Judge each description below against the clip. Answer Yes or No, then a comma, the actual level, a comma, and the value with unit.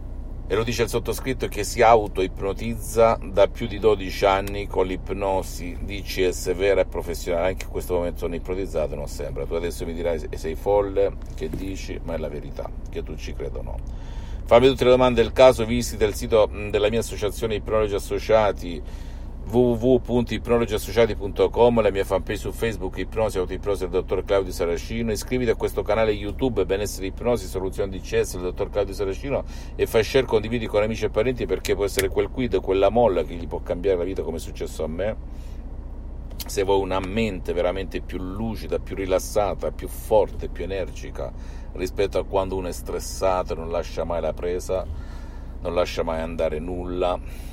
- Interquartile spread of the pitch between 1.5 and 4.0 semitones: No, average, 4.9 semitones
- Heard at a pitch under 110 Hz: Yes, very low, 95 Hz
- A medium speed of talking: No, fast, 180 wpm